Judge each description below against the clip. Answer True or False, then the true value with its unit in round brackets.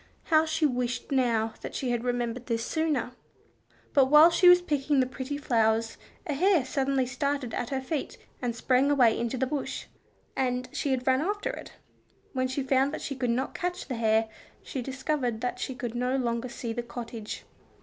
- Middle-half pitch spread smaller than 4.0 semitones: True (2.9 semitones)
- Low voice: False (260 Hz)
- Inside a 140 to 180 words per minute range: False (190 wpm)